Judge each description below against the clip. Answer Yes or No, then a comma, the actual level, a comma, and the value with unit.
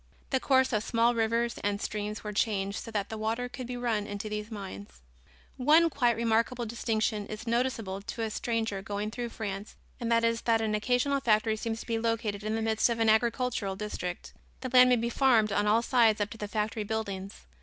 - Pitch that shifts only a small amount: Yes, narrow, 2.1 semitones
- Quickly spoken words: Yes, fast, 210 wpm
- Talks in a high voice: Yes, high, 225 Hz